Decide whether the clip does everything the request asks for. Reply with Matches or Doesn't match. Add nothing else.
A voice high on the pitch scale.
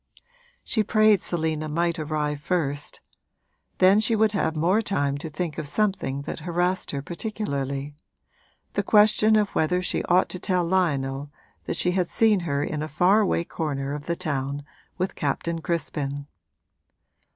Doesn't match